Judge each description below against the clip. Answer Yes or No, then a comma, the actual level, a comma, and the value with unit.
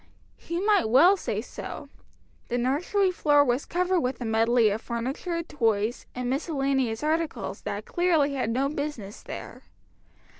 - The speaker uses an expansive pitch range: Yes, wide, 5.8 semitones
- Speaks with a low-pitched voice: No, very high, 275 Hz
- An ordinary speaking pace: Yes, average, 150 wpm